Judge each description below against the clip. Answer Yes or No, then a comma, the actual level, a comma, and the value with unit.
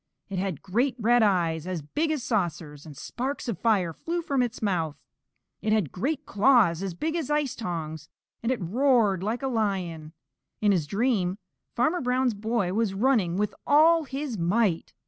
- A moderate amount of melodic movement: No, wide, 6.4 semitones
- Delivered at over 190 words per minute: No, average, 175 wpm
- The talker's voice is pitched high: Yes, high, 215 Hz